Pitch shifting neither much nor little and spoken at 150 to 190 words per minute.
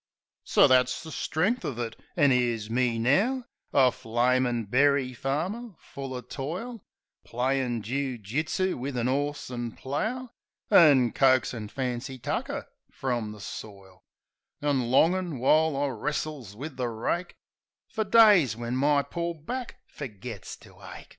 No: average, 4.5 semitones; average, 140 wpm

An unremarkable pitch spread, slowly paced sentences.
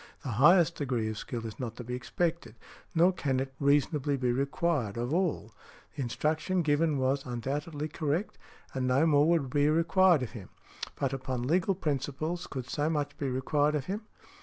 No: average, 3.9 semitones; average, 180 wpm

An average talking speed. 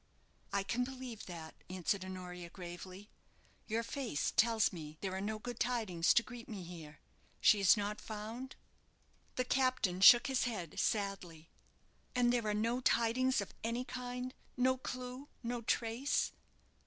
Yes: average, 150 wpm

